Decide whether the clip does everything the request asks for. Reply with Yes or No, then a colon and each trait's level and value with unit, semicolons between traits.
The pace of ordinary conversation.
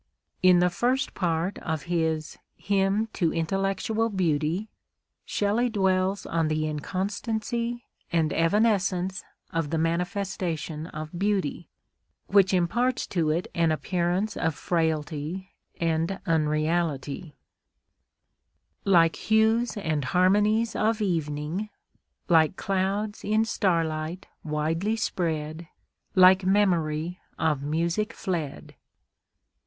No: slow, 100 wpm